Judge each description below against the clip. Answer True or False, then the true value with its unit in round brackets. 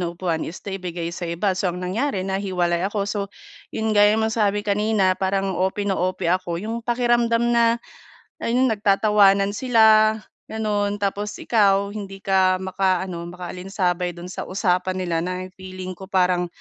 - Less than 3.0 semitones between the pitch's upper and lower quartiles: True (2.5 semitones)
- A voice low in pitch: False (195 Hz)